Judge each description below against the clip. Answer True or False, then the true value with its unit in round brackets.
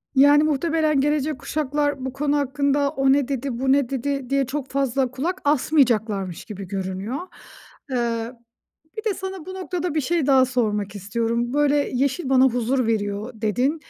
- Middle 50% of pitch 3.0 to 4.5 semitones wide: True (3.7 semitones)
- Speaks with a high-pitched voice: True (270 Hz)